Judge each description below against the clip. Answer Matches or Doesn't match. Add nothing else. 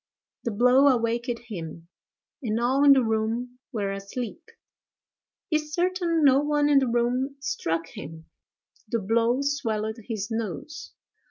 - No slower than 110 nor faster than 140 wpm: Matches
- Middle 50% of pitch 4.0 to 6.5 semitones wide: Matches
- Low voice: Doesn't match